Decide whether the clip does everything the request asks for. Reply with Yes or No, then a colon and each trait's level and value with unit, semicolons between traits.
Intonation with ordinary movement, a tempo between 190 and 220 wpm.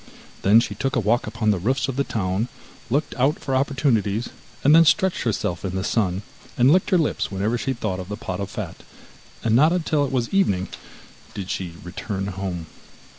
No: wide, 5.8 semitones; average, 200 wpm